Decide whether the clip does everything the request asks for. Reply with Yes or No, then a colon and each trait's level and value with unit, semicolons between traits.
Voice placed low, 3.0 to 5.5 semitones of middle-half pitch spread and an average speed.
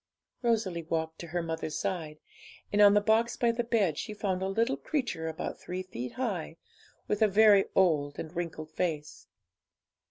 No: medium, 185 Hz; average, 5.2 semitones; average, 170 wpm